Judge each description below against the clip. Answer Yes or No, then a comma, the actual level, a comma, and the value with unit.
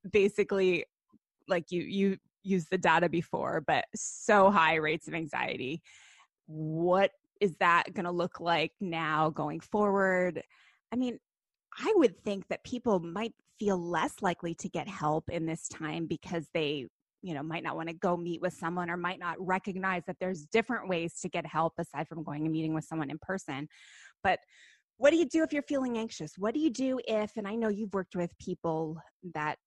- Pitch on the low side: No, medium, 180 Hz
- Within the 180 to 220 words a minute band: Yes, average, 190 wpm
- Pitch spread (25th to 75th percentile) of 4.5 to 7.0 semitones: No, average, 3.7 semitones